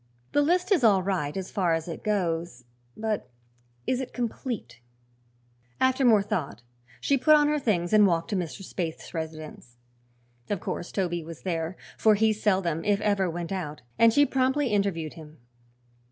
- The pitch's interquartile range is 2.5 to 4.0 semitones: No, average, 5.3 semitones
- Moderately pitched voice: No, high, 195 Hz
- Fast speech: No, average, 170 wpm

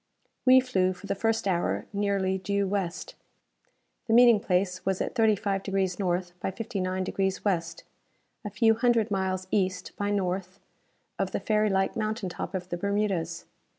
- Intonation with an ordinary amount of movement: No, narrow, 2.3 semitones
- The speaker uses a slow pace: No, average, 155 wpm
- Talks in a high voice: Yes, high, 195 Hz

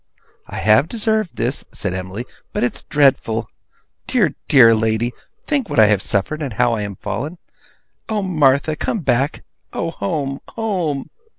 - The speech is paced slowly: No, average, 155 wpm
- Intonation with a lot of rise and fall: Yes, wide, 6.8 semitones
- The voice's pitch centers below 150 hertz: Yes, low, 135 Hz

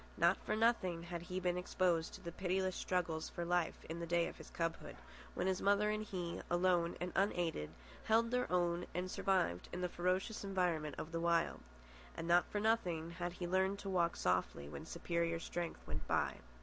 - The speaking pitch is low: No, medium, 175 Hz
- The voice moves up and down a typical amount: No, narrow, 1.9 semitones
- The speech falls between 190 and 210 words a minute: Yes, average, 195 wpm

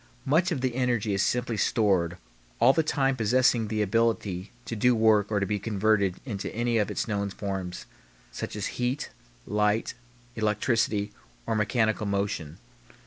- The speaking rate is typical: Yes, average, 155 wpm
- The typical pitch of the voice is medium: No, low, 110 Hz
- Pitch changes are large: No, average, 3.0 semitones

